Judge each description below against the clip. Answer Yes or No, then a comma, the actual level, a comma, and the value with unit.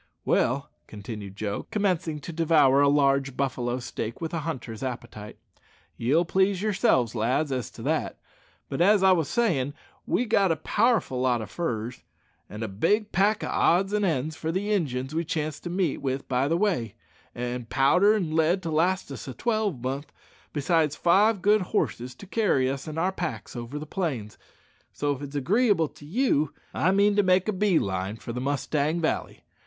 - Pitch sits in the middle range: Yes, medium, 155 Hz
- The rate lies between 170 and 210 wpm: Yes, average, 185 wpm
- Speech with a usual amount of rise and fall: No, wide, 6.6 semitones